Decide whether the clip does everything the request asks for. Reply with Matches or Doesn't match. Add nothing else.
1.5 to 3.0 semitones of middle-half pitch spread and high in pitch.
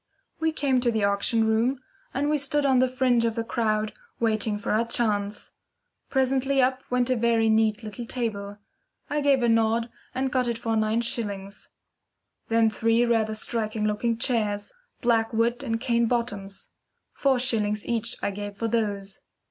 Matches